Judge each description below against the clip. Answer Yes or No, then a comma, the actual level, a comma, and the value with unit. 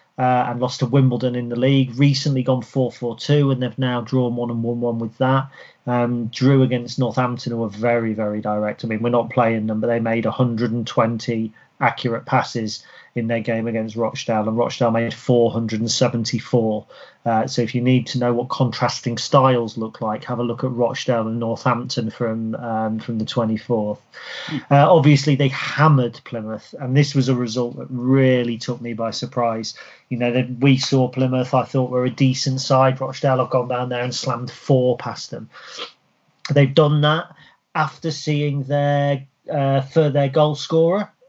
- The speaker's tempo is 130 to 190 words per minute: Yes, average, 180 wpm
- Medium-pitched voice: No, low, 125 Hz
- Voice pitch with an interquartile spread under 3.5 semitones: Yes, narrow, 2.4 semitones